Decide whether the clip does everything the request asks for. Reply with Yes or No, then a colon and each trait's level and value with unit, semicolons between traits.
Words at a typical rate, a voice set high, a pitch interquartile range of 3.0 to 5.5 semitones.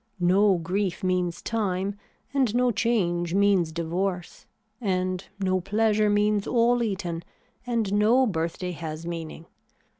No: slow, 120 wpm; high, 195 Hz; average, 3.5 semitones